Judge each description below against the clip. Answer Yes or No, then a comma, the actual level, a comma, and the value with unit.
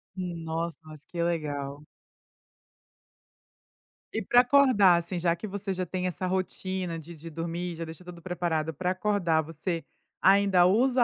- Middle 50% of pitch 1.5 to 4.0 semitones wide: Yes, narrow, 2.4 semitones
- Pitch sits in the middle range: Yes, medium, 175 Hz